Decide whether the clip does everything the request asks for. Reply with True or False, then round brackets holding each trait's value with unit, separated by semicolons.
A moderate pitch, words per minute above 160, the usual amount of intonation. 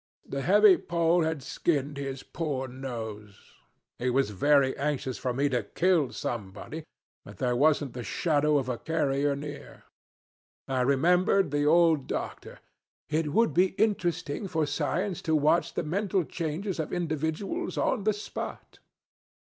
False (150 Hz; 145 wpm; 4.3 semitones)